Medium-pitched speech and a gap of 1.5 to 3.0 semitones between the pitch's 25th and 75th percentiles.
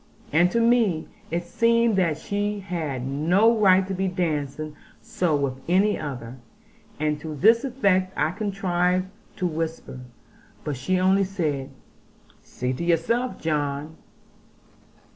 No: medium, 175 Hz; average, 4.6 semitones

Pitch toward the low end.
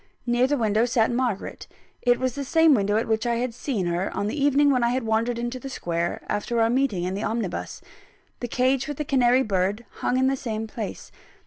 No: high, 240 Hz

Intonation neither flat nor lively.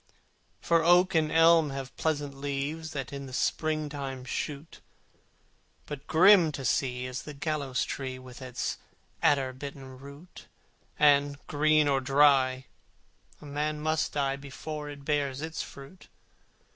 No: narrow, 2.2 semitones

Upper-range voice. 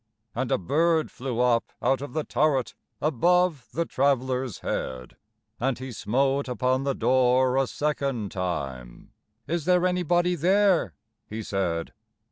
No: low, 130 Hz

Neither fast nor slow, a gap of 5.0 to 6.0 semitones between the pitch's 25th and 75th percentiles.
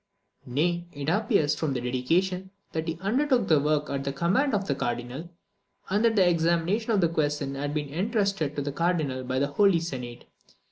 Yes: average, 190 wpm; average, 5.3 semitones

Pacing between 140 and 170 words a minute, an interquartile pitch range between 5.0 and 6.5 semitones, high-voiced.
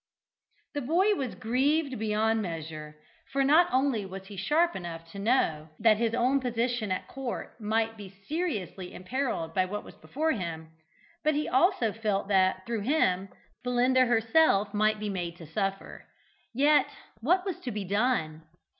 Yes: average, 160 wpm; wide, 5.6 semitones; high, 220 Hz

